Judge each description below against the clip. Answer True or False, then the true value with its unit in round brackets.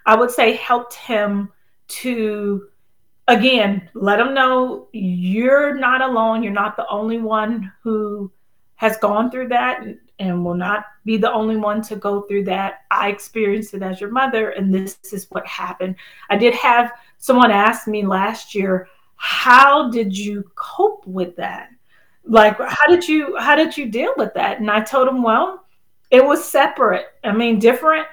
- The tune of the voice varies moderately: True (3.8 semitones)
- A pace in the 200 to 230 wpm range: False (175 wpm)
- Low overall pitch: False (220 Hz)